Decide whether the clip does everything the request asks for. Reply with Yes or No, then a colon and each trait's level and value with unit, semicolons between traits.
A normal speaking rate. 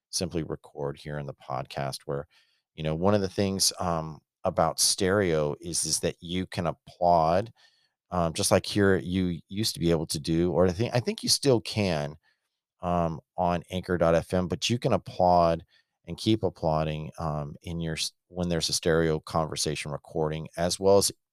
Yes: average, 175 wpm